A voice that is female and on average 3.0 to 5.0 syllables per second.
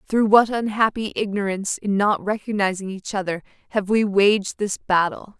Yes: female; 4.8 syllables/s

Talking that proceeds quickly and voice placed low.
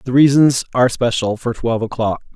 No: average, 180 wpm; low, 120 Hz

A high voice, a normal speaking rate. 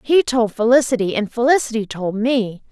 Yes: high, 235 Hz; average, 155 wpm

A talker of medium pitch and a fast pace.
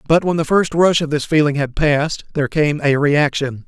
Yes: medium, 150 Hz; fast, 230 wpm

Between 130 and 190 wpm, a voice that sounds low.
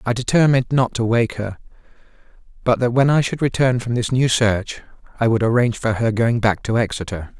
No: fast, 205 wpm; low, 120 Hz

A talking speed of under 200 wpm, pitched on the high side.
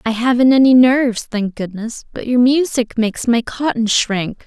Yes: average, 175 wpm; high, 240 Hz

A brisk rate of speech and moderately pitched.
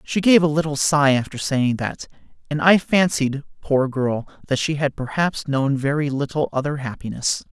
No: average, 175 wpm; medium, 145 Hz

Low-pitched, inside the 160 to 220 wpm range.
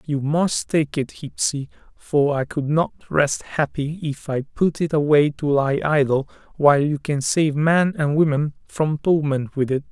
No: medium, 145 Hz; average, 180 wpm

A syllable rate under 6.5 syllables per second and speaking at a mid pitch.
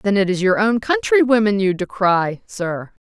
No: 4.6 syllables/s; high, 195 Hz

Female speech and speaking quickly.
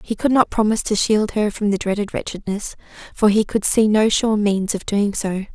Yes: female; fast, 225 wpm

